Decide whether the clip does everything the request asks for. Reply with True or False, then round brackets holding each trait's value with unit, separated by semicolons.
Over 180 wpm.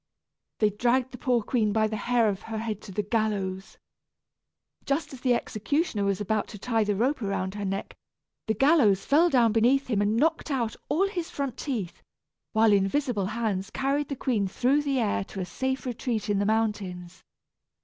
True (190 wpm)